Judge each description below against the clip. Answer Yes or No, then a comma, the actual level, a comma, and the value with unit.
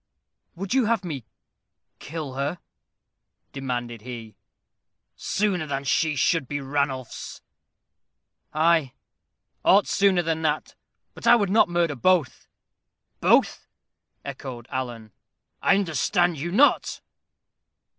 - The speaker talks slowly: Yes, slow, 105 wpm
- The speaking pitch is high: No, medium, 155 Hz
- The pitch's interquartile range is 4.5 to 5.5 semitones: Yes, average, 5.2 semitones